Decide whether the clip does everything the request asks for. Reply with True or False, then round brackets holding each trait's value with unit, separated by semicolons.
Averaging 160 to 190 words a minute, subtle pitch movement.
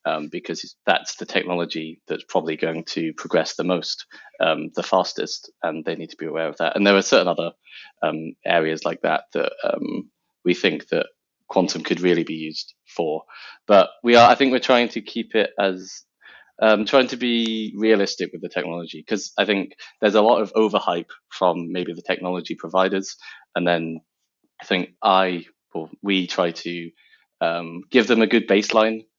False (185 wpm; 4.4 semitones)